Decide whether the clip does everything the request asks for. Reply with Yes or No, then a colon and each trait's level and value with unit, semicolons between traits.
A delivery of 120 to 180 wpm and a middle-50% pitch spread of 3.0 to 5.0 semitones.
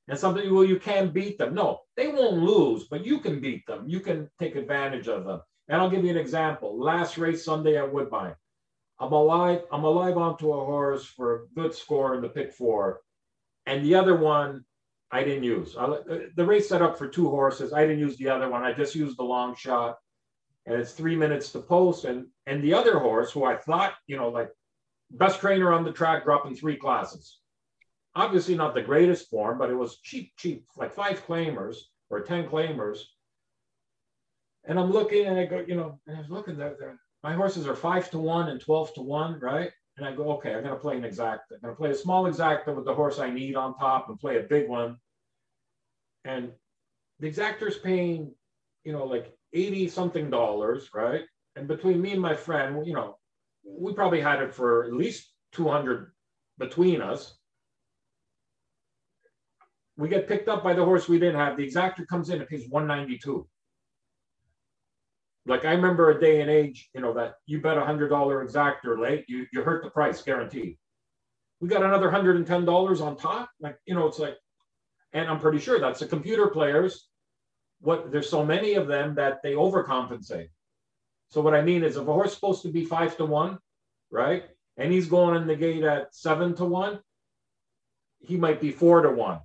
No: average, 200 wpm; average, 4.4 semitones